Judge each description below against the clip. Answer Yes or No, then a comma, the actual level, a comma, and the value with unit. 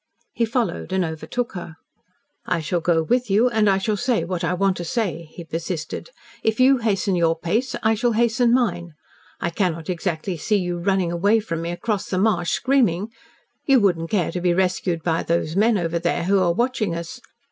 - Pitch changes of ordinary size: Yes, average, 4.6 semitones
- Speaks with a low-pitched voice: No, medium, 185 Hz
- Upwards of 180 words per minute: Yes, average, 200 wpm